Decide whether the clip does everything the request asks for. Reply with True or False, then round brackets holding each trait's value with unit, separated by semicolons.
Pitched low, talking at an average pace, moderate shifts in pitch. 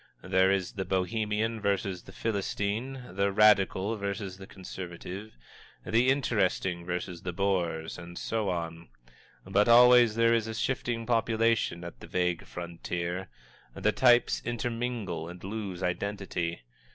False (100 Hz; 130 wpm; 4.1 semitones)